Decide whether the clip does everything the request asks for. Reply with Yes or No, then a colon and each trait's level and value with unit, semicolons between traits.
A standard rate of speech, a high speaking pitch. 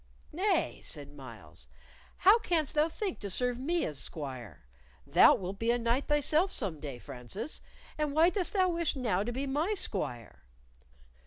Yes: average, 165 wpm; very high, 250 Hz